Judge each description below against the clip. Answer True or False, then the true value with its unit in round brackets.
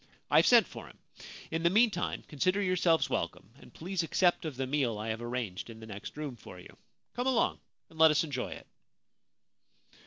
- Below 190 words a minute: False (195 wpm)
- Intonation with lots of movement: True (7.0 semitones)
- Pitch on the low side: False (150 Hz)